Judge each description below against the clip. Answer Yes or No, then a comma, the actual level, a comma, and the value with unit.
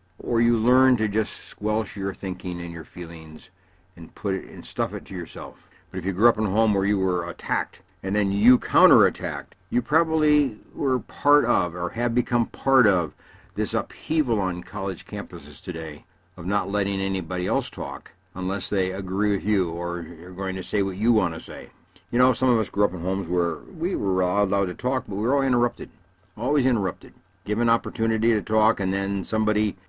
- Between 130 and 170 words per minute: No, fast, 205 wpm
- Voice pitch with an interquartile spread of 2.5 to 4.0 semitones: Yes, average, 3.7 semitones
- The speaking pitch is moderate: No, low, 100 Hz